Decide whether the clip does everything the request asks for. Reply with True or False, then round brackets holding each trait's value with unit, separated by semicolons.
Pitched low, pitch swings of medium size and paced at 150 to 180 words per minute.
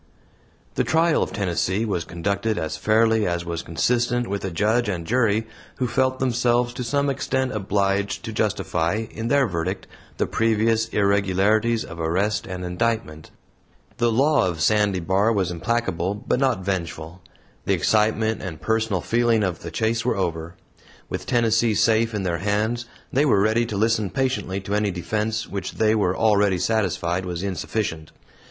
True (105 Hz; 3.8 semitones; 160 wpm)